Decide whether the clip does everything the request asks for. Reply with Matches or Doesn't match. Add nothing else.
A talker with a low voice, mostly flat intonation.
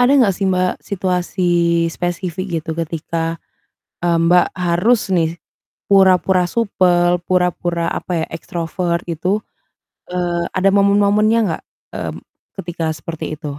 Doesn't match